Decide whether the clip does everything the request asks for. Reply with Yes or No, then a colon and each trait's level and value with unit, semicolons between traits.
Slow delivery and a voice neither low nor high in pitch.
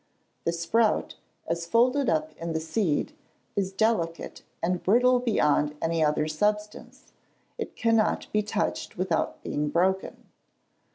Yes: slow, 125 wpm; medium, 180 Hz